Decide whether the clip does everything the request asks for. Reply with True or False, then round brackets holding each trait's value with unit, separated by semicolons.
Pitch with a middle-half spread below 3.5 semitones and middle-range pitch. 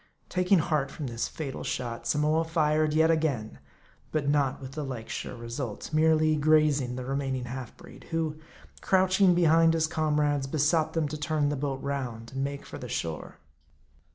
True (2.9 semitones; 150 Hz)